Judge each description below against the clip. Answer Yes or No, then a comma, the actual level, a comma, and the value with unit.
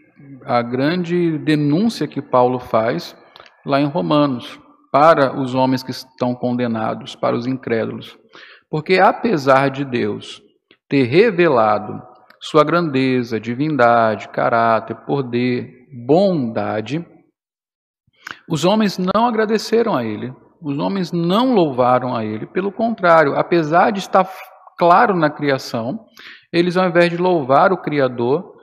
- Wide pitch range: Yes, wide, 6.1 semitones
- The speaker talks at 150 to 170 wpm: No, slow, 120 wpm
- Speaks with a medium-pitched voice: Yes, medium, 145 Hz